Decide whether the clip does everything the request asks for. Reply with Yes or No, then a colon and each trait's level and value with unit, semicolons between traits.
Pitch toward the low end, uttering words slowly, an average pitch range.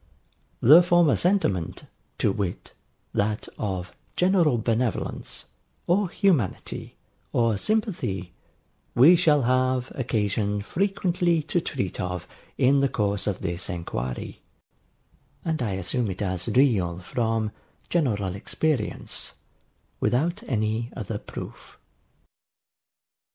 No: low, 115 Hz; slow, 105 wpm; wide, 8.0 semitones